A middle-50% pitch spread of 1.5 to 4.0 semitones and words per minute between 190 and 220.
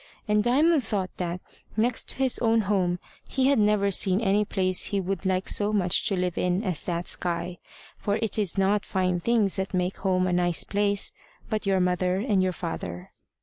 Yes: narrow, 2.6 semitones; average, 195 wpm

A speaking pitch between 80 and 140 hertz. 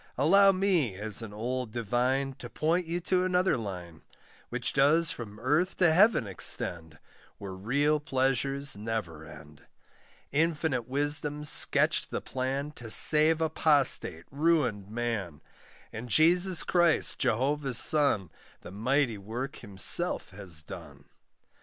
Yes: low, 135 Hz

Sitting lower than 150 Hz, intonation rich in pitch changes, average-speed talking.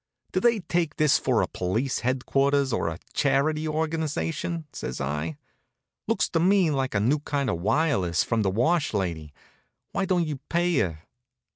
Yes: medium, 140 Hz; wide, 8.1 semitones; average, 160 wpm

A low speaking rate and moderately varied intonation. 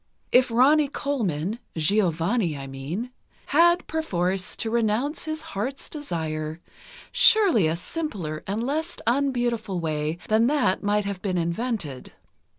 No: slow, 115 wpm; wide, 8.3 semitones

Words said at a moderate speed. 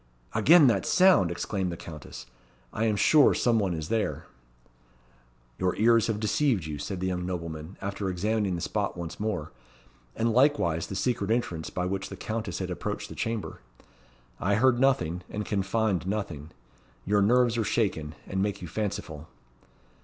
Yes: average, 170 wpm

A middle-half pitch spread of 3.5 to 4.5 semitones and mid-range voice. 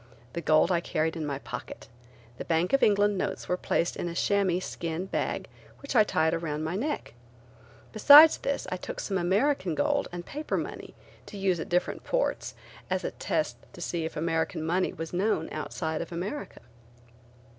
Yes: average, 4.0 semitones; medium, 175 Hz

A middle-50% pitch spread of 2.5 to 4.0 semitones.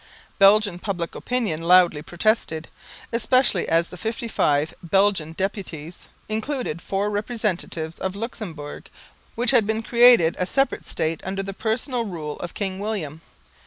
No: average, 4.9 semitones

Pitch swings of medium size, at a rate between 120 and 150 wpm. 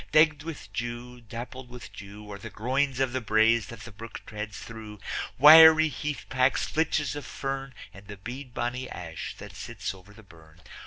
No: average, 4.4 semitones; average, 170 wpm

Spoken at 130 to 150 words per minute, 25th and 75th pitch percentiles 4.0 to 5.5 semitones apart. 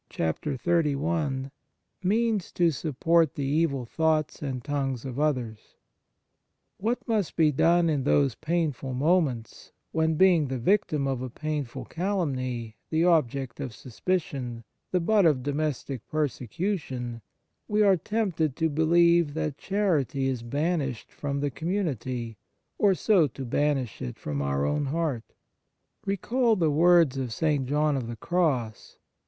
Yes: slow, 135 wpm; average, 4.7 semitones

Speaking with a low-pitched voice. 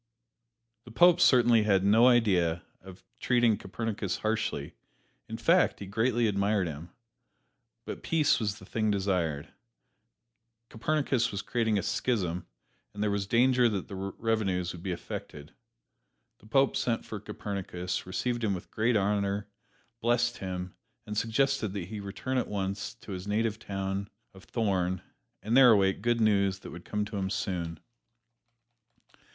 Yes: low, 105 Hz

